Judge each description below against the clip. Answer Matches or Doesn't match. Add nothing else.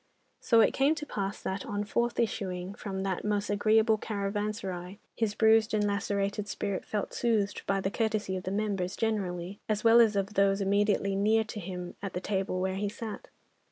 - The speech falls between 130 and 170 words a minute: Doesn't match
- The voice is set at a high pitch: Matches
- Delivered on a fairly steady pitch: Matches